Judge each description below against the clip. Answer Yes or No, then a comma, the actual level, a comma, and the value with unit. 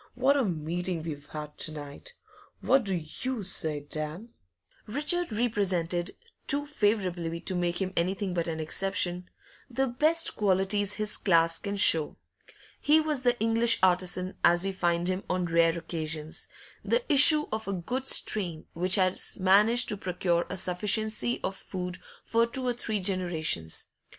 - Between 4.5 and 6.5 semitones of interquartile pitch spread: Yes, average, 4.9 semitones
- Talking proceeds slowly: No, average, 155 wpm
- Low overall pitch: No, medium, 185 Hz